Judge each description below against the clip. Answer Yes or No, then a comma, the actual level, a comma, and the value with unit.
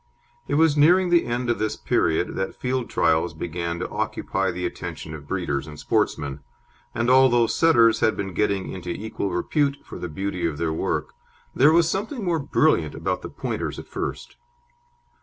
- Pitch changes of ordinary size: No, wide, 8.5 semitones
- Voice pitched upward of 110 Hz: No, low, 105 Hz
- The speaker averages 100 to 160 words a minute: No, average, 175 wpm